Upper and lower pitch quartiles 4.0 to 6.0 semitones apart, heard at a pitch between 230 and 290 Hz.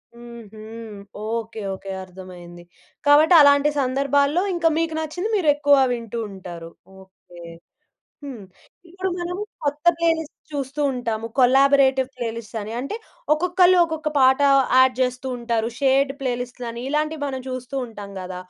Yes: average, 4.5 semitones; very high, 260 Hz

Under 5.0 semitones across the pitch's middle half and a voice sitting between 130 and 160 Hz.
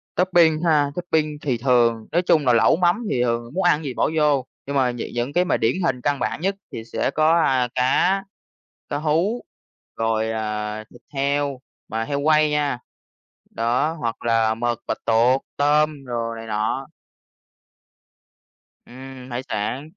Yes: average, 4.6 semitones; low, 135 Hz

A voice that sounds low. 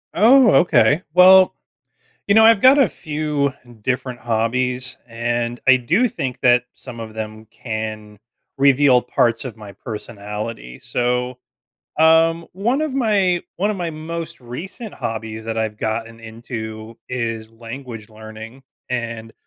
Yes: low, 125 Hz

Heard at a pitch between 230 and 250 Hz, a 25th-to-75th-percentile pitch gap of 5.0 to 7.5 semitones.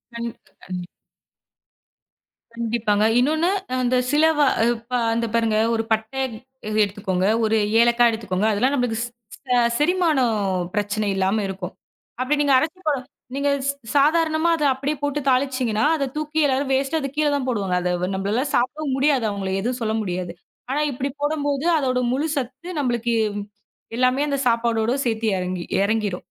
No: high, 245 Hz; average, 4.5 semitones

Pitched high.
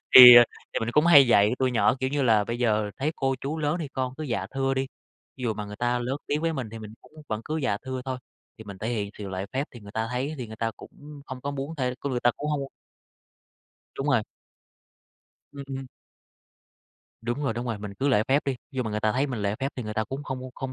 No: low, 125 Hz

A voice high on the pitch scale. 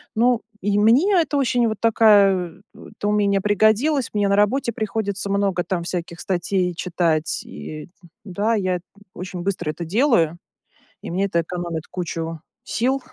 Yes: high, 200 Hz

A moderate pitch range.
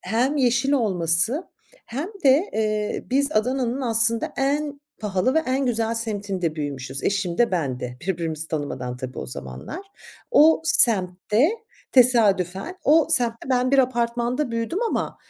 No: wide, 6.6 semitones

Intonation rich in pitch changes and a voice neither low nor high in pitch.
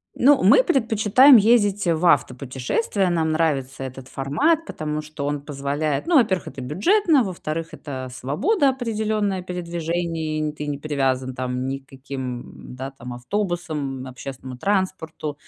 Yes: wide, 7.1 semitones; medium, 155 Hz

